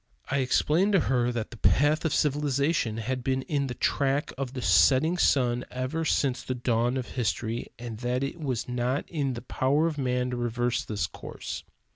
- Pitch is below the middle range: Yes, low, 130 Hz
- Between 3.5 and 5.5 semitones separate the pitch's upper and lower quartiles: No, average, 2.7 semitones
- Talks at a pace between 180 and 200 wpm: Yes, average, 190 wpm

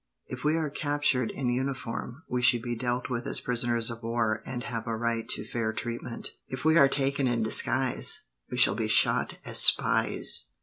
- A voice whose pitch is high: No, low, 120 Hz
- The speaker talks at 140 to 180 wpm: No, average, 190 wpm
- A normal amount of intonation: No, narrow, 2.3 semitones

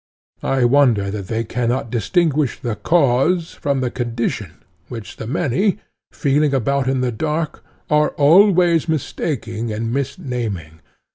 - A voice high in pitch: No, low, 130 Hz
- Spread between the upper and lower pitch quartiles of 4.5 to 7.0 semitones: Yes, average, 4.8 semitones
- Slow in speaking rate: Yes, slow, 130 wpm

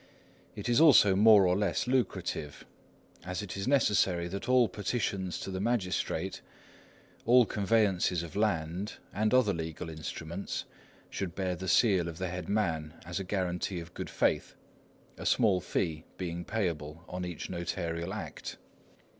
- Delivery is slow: No, average, 150 wpm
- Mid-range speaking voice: No, very low, 95 Hz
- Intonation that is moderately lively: Yes, average, 3.5 semitones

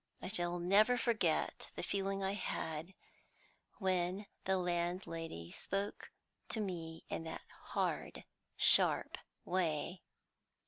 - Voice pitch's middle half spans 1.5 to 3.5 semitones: Yes, average, 2.8 semitones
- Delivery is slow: Yes, slow, 105 wpm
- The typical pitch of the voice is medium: Yes, medium, 180 Hz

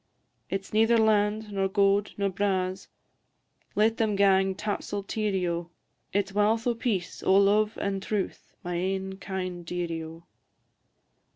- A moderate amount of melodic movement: No, narrow, 1.9 semitones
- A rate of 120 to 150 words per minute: Yes, average, 145 wpm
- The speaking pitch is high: Yes, high, 195 Hz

